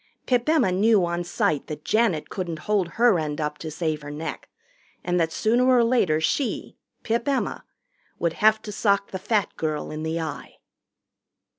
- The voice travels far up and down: Yes, wide, 6.0 semitones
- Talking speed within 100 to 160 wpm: No, average, 175 wpm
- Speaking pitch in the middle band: Yes, medium, 180 Hz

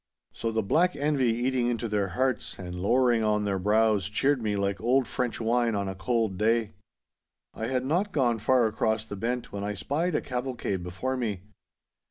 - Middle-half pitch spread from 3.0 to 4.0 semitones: Yes, average, 3.6 semitones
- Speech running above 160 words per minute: Yes, average, 190 wpm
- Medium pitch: No, low, 115 Hz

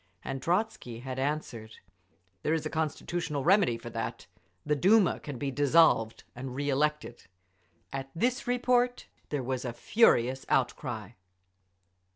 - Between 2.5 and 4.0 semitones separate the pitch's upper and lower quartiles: No, average, 5.2 semitones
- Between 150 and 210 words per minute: No, slow, 135 wpm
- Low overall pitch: No, medium, 145 Hz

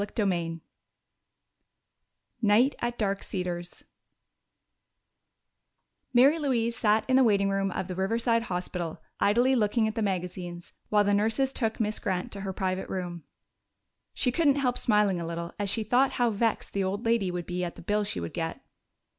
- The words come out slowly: No, average, 170 wpm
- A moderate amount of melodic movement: Yes, average, 4.2 semitones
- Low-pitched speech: No, high, 205 Hz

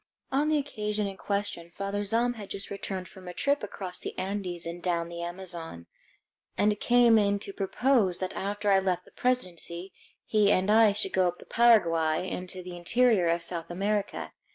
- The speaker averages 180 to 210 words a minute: Yes, average, 185 wpm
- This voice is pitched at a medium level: No, high, 195 Hz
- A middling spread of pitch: Yes, average, 3.1 semitones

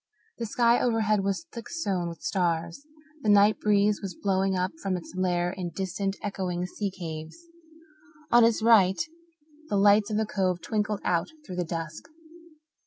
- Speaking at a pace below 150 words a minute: No, average, 165 wpm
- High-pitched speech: Yes, high, 195 Hz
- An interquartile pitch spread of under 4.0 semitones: Yes, average, 3.0 semitones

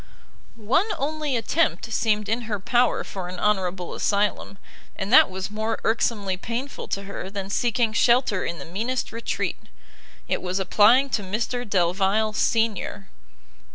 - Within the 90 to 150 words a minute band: Yes, average, 145 wpm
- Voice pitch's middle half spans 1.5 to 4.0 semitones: Yes, average, 3.5 semitones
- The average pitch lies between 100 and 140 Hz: No, high, 210 Hz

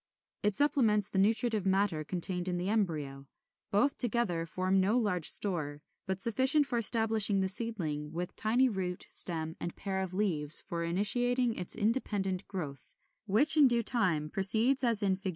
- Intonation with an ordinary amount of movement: Yes, average, 4.4 semitones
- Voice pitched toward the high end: Yes, high, 195 Hz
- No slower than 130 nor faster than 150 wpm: No, average, 165 wpm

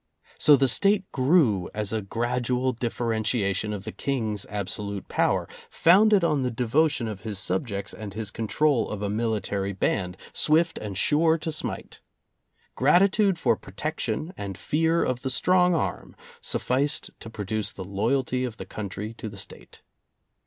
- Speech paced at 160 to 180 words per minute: No, average, 150 wpm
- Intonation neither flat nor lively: No, wide, 6.6 semitones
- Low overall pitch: Yes, low, 115 Hz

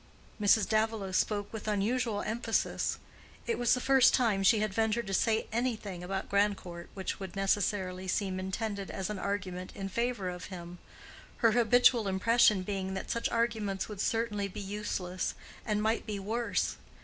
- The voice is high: Yes, high, 205 Hz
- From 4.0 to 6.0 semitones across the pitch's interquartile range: No, average, 2.8 semitones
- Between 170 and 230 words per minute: No, average, 160 wpm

